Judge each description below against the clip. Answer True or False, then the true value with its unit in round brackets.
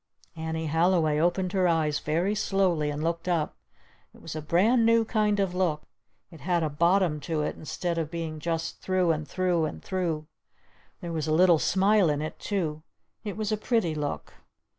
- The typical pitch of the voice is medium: True (170 Hz)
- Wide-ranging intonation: False (3.3 semitones)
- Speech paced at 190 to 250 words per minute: True (195 wpm)